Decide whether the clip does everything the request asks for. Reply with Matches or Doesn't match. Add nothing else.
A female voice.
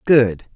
Matches